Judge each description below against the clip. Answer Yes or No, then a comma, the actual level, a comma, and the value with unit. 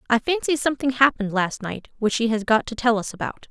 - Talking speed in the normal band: No, fast, 240 wpm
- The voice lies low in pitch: No, high, 235 Hz